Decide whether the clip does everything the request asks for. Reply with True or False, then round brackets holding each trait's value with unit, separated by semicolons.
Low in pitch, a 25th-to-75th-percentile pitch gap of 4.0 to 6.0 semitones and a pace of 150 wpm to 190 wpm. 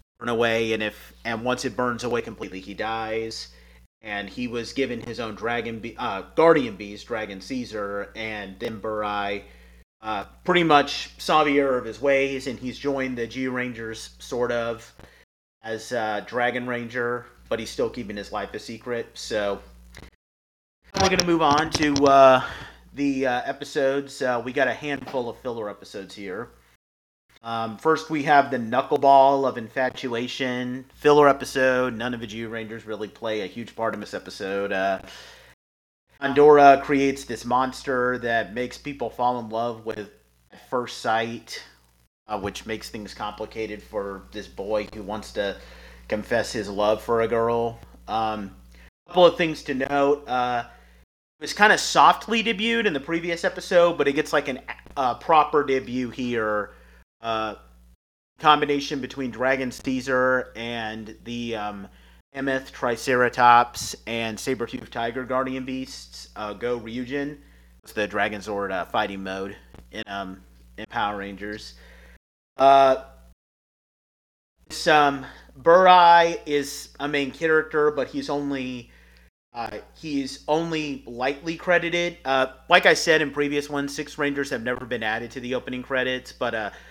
True (120 Hz; 4.8 semitones; 155 wpm)